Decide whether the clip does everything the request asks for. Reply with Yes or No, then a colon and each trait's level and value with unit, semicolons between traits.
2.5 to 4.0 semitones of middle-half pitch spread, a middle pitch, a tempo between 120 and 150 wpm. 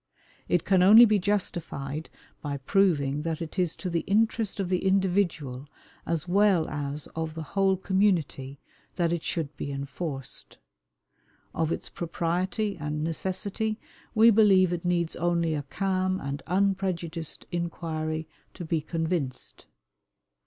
Yes: average, 3.6 semitones; medium, 170 Hz; slow, 135 wpm